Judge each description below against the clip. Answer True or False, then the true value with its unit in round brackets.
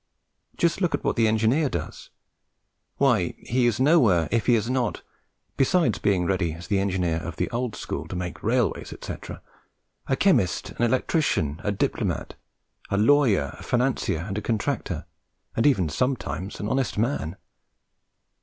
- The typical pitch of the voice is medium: False (110 Hz)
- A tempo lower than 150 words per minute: False (155 wpm)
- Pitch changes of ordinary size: False (6.1 semitones)